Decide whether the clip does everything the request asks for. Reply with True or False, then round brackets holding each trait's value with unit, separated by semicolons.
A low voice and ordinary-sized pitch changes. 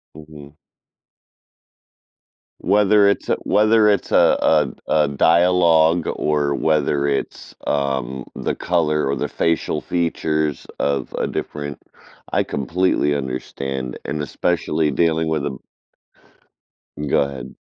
True (75 Hz; 3.2 semitones)